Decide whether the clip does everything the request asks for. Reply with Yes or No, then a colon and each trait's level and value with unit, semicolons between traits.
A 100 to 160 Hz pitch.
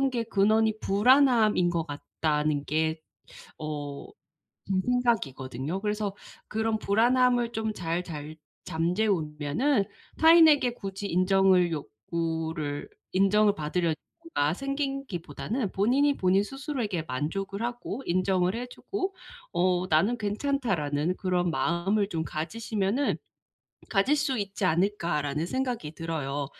No: high, 195 Hz